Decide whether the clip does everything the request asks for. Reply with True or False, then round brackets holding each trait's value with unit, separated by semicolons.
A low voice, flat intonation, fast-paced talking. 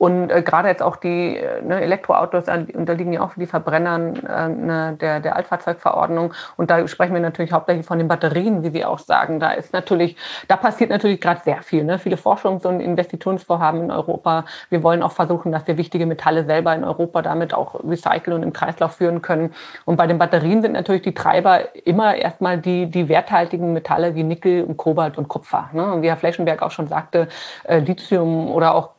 False (170 Hz; 1.5 semitones; 205 wpm)